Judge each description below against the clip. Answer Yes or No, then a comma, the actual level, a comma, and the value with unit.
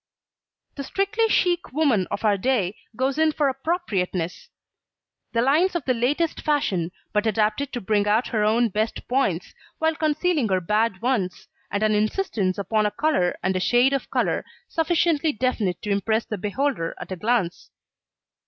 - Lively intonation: Yes, wide, 6.4 semitones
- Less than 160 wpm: No, average, 165 wpm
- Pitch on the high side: Yes, high, 230 Hz